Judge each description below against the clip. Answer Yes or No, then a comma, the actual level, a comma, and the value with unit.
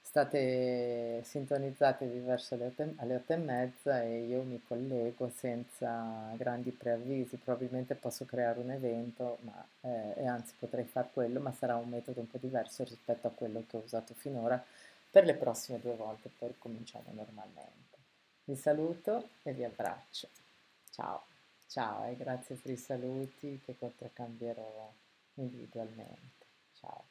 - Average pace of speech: Yes, average, 140 wpm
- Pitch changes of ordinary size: No, narrow, 1.6 semitones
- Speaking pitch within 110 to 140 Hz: Yes, low, 125 Hz